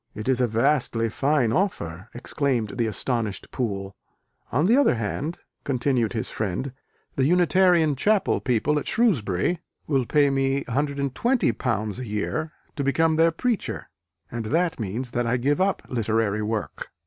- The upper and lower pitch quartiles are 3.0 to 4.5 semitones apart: No, wide, 5.4 semitones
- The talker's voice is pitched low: Yes, low, 130 Hz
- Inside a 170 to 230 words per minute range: No, average, 150 wpm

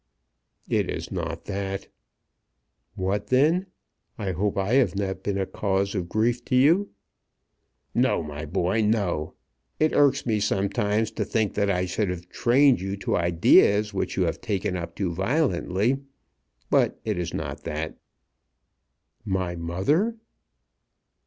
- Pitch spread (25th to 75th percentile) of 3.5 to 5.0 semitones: Yes, average, 4.1 semitones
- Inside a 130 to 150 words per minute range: Yes, average, 140 wpm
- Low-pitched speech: Yes, low, 100 Hz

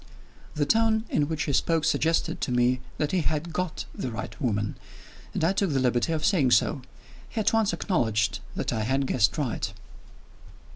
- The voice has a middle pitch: Yes, medium, 145 Hz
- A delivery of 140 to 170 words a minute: No, average, 185 wpm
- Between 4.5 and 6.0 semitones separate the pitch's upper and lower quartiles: Yes, wide, 5.6 semitones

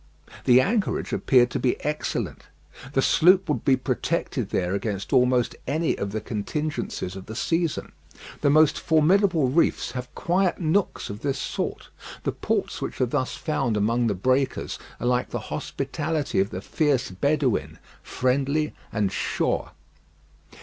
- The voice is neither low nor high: No, low, 130 Hz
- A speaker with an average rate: Yes, average, 150 wpm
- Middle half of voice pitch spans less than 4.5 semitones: No, average, 4.8 semitones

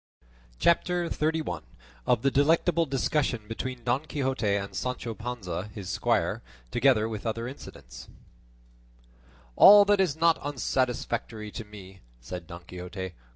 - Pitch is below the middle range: Yes, low, 120 Hz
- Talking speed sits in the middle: No, slow, 125 wpm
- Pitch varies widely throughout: Yes, wide, 6.0 semitones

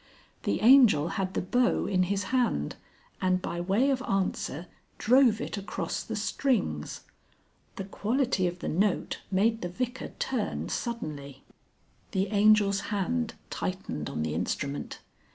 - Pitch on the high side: Yes, high, 195 Hz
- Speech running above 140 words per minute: No, slow, 135 wpm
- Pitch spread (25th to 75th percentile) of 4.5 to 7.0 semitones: Yes, average, 5.0 semitones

